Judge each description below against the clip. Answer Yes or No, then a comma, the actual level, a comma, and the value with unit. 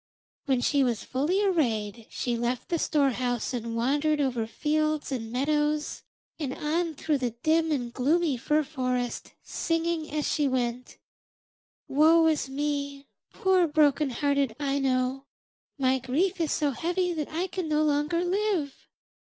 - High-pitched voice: Yes, very high, 290 Hz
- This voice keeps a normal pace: Yes, average, 145 wpm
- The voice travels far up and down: No, average, 3.6 semitones